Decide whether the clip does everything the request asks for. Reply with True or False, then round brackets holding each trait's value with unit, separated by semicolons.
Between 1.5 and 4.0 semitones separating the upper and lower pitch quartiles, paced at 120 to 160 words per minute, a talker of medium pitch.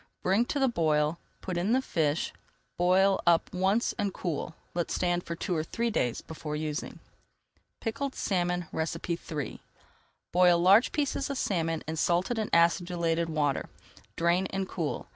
True (3.0 semitones; 150 wpm; 175 Hz)